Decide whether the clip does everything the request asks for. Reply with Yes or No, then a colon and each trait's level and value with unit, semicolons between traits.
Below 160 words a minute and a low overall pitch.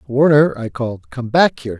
No: average, 200 wpm; low, 125 Hz